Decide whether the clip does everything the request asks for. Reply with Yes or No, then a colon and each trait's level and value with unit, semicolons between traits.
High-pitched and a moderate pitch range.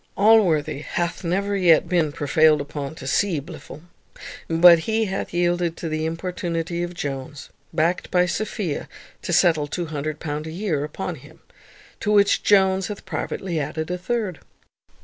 No: medium, 170 Hz; average, 3.2 semitones